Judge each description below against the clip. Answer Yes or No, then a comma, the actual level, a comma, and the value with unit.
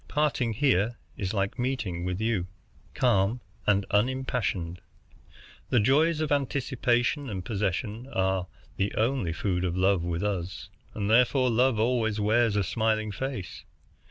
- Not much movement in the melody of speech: No, average, 4.7 semitones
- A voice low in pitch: Yes, low, 110 Hz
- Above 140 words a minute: No, slow, 135 wpm